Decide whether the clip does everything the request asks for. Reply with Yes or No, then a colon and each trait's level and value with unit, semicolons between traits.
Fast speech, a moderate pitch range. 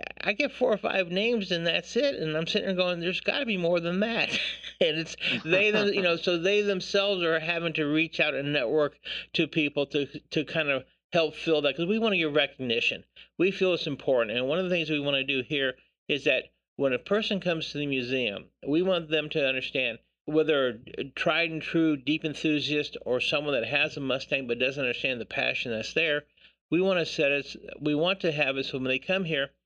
Yes: fast, 235 wpm; average, 4.0 semitones